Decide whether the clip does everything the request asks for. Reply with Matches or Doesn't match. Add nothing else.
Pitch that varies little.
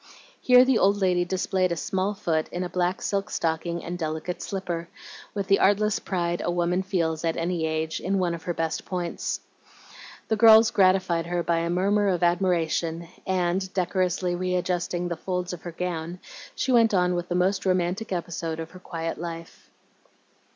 Matches